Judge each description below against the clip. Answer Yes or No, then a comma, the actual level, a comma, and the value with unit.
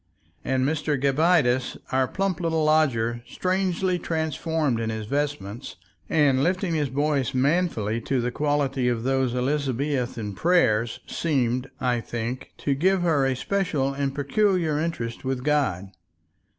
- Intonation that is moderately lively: Yes, average, 4.3 semitones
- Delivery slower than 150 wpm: Yes, slow, 135 wpm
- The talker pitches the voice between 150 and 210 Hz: No, medium, 140 Hz